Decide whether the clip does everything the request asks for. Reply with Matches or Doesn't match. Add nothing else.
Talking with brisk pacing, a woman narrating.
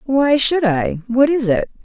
Doesn't match